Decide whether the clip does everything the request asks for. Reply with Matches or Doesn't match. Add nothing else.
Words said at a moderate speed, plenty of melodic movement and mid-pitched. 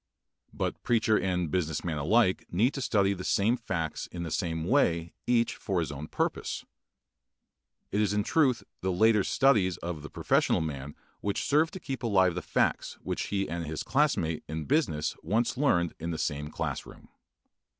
Doesn't match